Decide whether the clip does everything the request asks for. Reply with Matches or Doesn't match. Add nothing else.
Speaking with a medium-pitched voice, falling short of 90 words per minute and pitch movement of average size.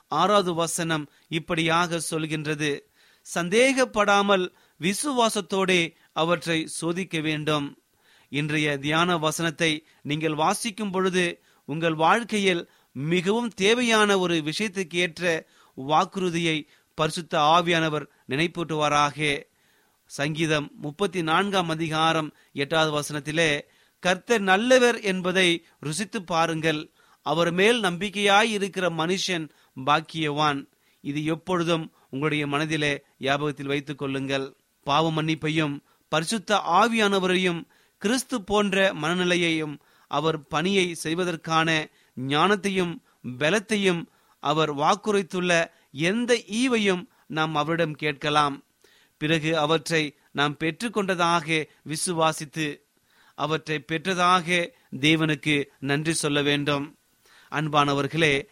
Matches